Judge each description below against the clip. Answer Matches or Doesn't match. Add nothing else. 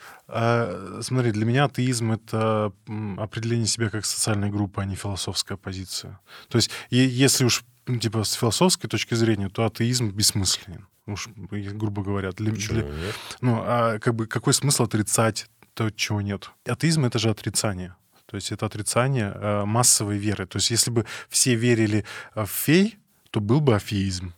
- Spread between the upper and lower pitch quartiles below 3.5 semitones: Matches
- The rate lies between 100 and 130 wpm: Doesn't match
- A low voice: Matches